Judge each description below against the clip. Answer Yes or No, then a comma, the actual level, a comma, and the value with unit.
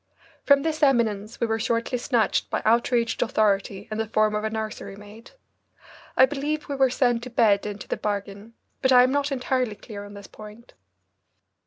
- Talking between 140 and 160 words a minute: No, average, 185 wpm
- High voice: Yes, high, 225 Hz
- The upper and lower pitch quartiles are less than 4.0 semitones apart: Yes, average, 3.3 semitones